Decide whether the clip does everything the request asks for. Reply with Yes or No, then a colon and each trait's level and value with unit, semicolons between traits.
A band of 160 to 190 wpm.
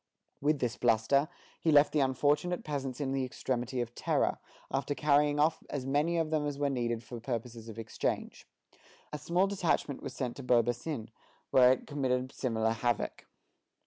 Yes: average, 170 wpm